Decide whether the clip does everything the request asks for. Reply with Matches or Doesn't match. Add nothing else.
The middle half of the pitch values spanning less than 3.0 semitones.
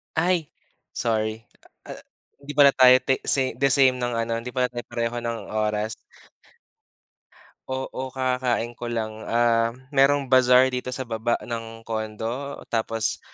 Matches